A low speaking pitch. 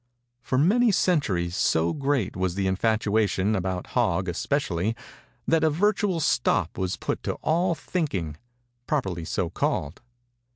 Yes: low, 110 Hz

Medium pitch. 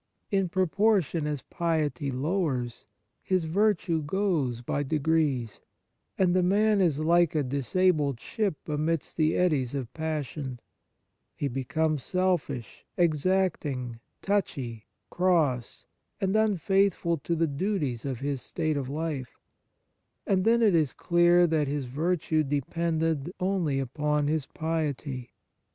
Yes: medium, 155 Hz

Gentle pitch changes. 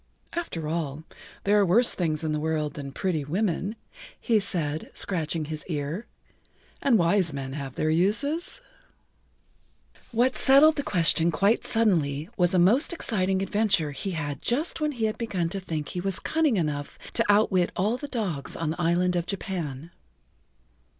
No: wide, 5.6 semitones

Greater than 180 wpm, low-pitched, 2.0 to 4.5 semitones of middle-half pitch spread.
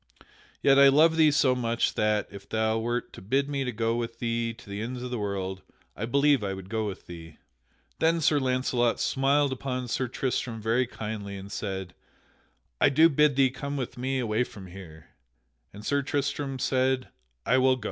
Yes: average, 190 wpm; low, 125 Hz; average, 4.1 semitones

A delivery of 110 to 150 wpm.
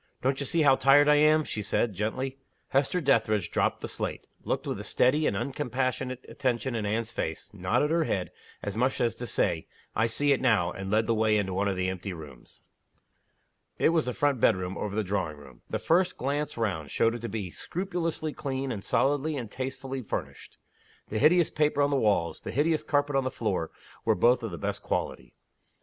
No: fast, 205 wpm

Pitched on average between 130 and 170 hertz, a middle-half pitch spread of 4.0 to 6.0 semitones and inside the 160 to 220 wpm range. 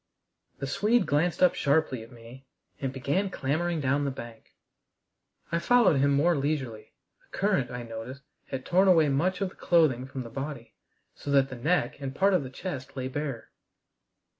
Yes: medium, 140 Hz; average, 4.8 semitones; average, 180 wpm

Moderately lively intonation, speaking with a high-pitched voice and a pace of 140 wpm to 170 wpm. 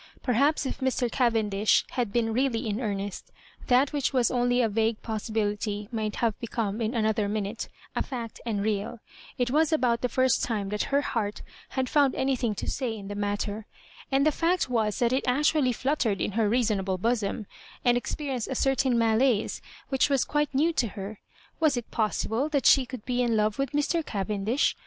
No: average, 3.7 semitones; high, 235 Hz; average, 190 wpm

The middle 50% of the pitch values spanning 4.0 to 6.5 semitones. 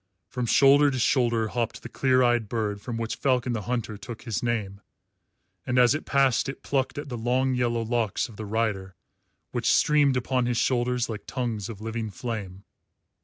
No: narrow, 2.5 semitones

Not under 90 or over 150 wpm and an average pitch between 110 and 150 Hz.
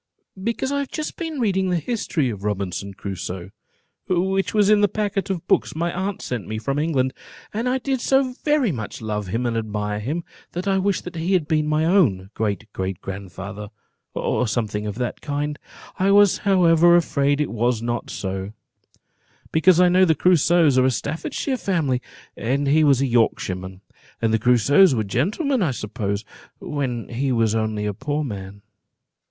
No: average, 180 wpm; medium, 140 Hz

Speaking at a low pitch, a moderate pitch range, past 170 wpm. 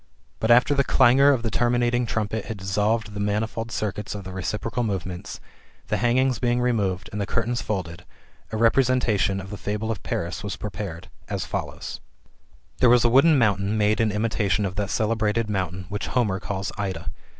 Yes: low, 105 Hz; average, 3.2 semitones; average, 185 wpm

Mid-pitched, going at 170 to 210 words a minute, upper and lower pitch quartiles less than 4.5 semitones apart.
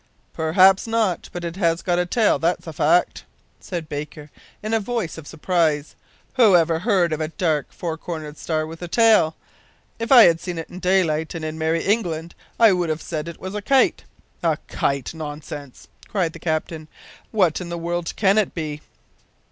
Yes: medium, 170 Hz; average, 190 wpm; average, 3.1 semitones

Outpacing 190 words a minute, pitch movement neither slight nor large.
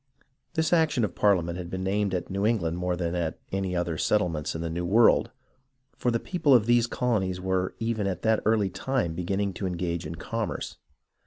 Yes: average, 200 wpm; average, 4.3 semitones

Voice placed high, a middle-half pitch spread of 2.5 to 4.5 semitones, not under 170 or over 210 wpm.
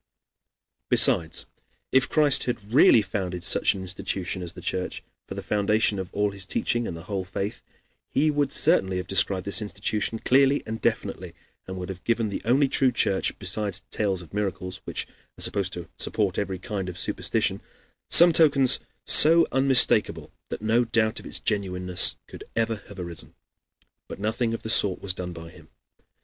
No: low, 100 Hz; average, 4.0 semitones; average, 175 wpm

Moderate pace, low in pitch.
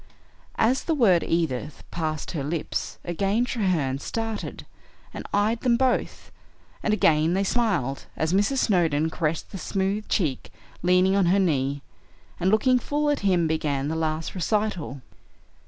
No: average, 145 wpm; medium, 180 Hz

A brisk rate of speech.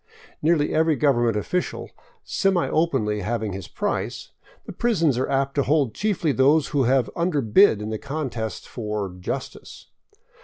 No: average, 155 wpm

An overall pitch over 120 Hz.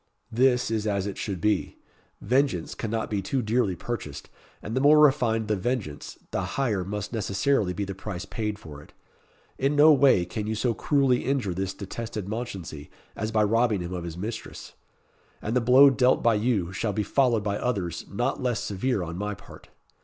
No: low, 110 Hz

